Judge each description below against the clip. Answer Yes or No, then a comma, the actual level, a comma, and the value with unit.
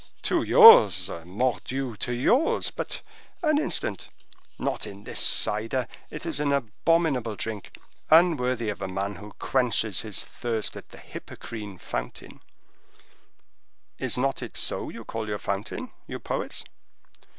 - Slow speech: Yes, slow, 125 wpm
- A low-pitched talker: Yes, low, 120 Hz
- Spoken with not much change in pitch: No, average, 5.2 semitones